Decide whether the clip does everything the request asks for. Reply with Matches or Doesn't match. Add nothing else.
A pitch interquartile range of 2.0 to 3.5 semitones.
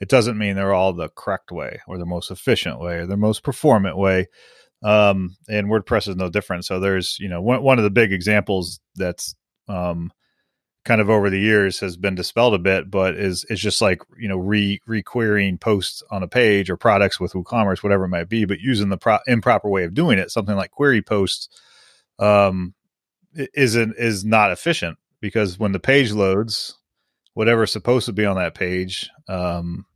Matches